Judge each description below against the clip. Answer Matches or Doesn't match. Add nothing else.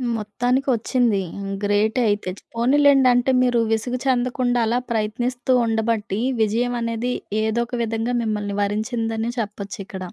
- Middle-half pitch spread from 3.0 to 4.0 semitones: Doesn't match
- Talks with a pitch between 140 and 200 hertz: Doesn't match